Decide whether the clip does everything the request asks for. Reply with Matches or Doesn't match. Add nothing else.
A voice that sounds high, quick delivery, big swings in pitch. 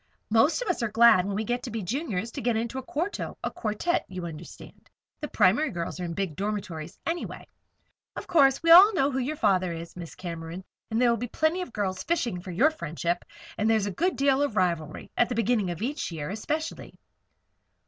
Matches